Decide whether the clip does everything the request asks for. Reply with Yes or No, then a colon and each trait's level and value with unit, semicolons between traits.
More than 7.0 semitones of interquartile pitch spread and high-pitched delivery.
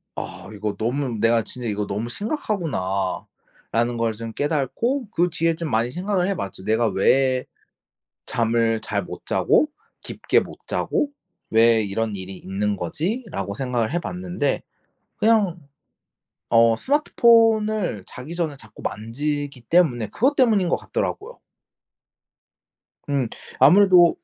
No: wide, 8.2 semitones; low, 130 Hz